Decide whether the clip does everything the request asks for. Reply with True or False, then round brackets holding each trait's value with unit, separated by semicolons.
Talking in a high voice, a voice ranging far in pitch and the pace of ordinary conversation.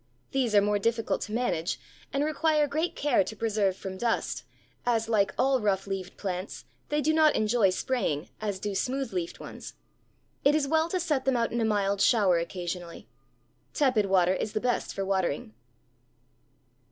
True (215 Hz; 5.7 semitones; 175 wpm)